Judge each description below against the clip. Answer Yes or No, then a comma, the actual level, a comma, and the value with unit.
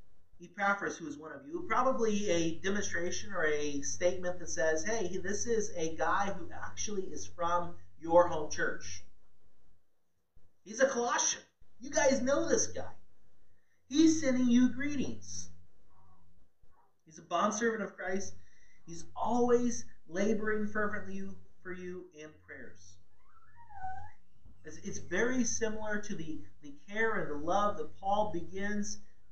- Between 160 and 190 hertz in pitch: Yes, medium, 185 Hz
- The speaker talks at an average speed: No, slow, 130 wpm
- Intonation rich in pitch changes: Yes, wide, 7.1 semitones